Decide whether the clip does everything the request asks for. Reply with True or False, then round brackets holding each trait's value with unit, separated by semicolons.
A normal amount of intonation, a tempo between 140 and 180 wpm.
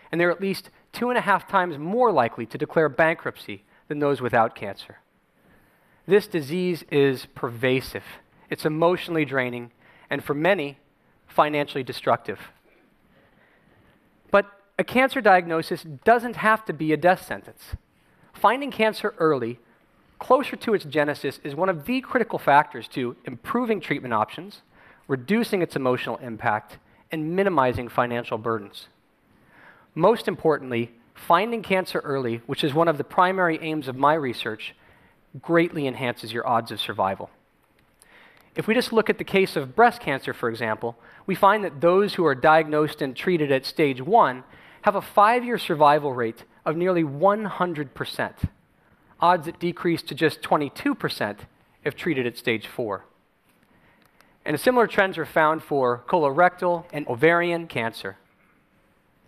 False (5.8 semitones; 145 wpm)